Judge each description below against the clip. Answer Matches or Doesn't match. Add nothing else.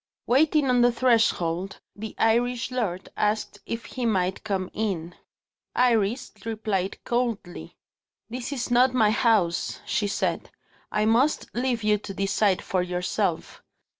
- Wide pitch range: Doesn't match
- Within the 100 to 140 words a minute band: Matches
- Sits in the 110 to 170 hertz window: Doesn't match